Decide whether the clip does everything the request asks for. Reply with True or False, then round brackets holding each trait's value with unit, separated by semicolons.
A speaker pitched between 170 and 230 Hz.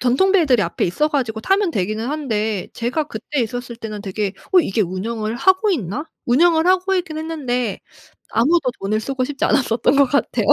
False (250 Hz)